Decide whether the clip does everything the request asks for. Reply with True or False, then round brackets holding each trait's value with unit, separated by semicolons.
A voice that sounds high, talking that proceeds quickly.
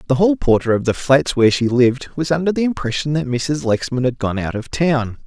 False (135 Hz; 240 wpm)